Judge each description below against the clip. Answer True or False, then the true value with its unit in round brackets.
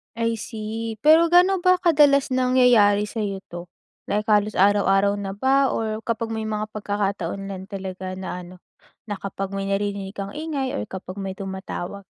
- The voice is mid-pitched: False (210 Hz)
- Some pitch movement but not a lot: True (3.5 semitones)